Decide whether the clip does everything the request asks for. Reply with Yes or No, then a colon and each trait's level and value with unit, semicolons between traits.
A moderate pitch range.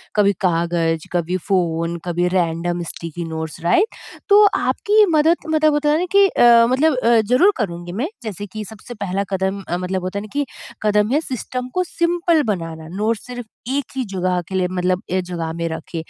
No: wide, 6.7 semitones